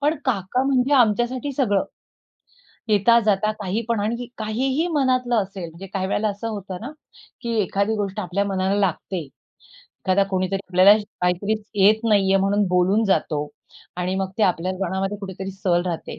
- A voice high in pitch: Yes, high, 200 Hz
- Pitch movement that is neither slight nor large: Yes, average, 3.2 semitones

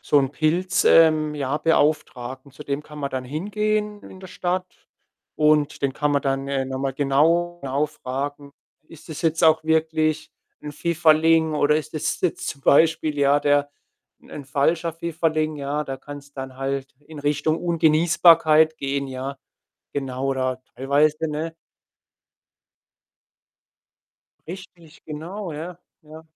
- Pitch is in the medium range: Yes, medium, 150 Hz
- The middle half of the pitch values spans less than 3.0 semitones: Yes, narrow, 2.6 semitones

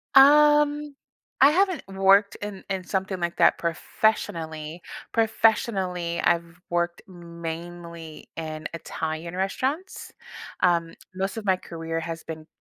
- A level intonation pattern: No, average, 4.2 semitones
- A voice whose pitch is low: No, medium, 180 Hz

